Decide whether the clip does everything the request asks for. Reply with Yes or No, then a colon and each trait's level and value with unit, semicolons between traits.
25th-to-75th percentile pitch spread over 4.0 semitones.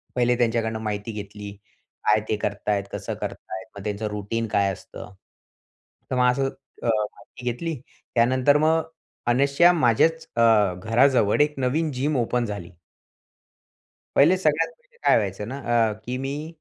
Yes: average, 4.9 semitones